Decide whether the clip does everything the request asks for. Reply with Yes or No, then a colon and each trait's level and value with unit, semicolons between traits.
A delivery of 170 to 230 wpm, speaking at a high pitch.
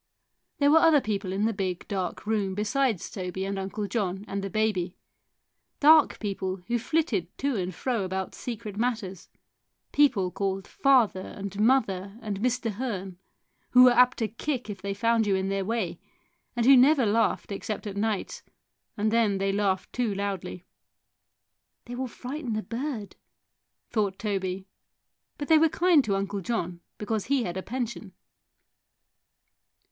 No: average, 160 wpm; high, 210 Hz